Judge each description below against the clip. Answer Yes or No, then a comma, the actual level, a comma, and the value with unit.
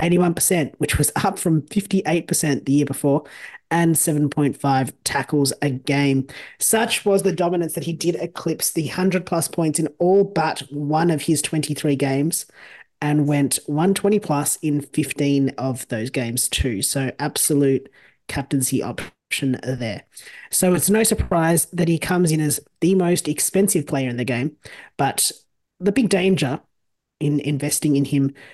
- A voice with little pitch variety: No, average, 3.7 semitones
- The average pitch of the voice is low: No, medium, 150 Hz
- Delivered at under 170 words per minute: Yes, average, 155 wpm